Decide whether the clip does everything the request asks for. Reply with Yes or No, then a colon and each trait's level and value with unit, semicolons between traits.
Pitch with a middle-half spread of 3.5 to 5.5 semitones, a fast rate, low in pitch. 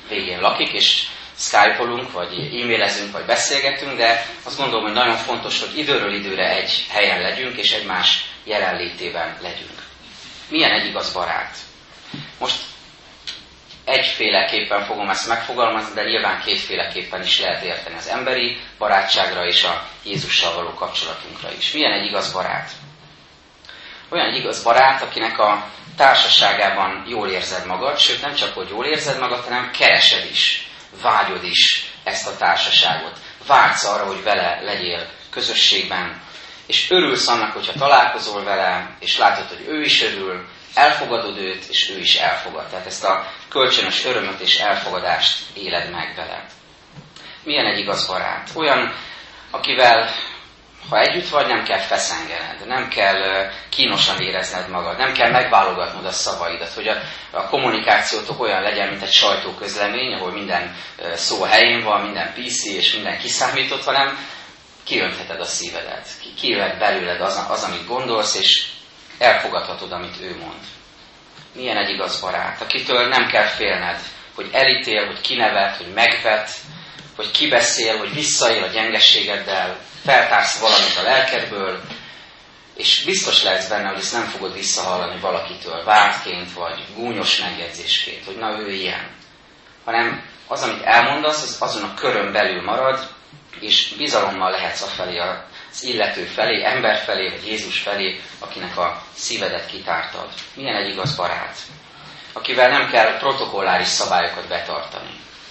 No: average, 4.5 semitones; average, 140 wpm; low, 110 Hz